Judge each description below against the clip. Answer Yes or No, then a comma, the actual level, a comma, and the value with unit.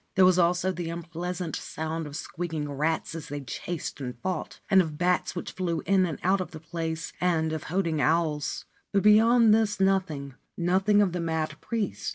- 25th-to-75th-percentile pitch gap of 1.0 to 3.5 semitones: Yes, average, 2.9 semitones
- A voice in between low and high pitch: Yes, medium, 170 Hz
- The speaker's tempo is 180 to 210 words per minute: Yes, average, 195 wpm